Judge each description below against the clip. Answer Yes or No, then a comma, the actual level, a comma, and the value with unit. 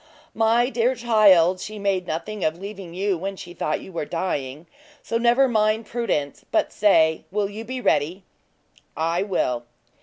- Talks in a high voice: Yes, high, 195 Hz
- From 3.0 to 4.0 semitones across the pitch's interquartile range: No, average, 4.8 semitones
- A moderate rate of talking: Yes, average, 160 wpm